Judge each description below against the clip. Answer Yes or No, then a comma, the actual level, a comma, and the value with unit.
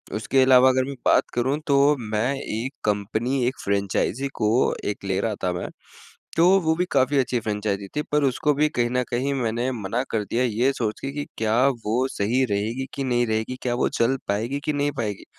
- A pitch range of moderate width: Yes, average, 3.8 semitones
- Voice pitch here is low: Yes, low, 120 Hz